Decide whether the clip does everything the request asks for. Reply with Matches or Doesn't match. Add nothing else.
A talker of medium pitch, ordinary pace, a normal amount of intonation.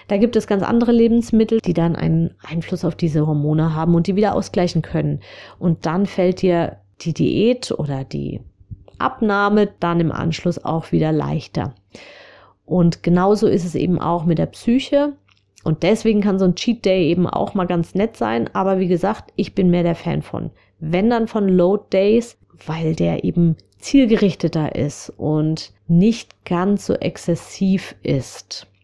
Matches